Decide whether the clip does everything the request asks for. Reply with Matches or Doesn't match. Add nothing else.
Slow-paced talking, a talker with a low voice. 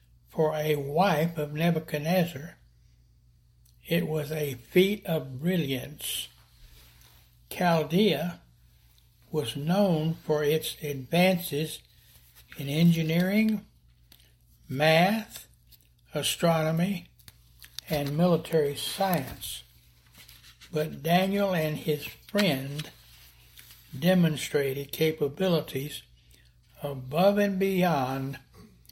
Doesn't match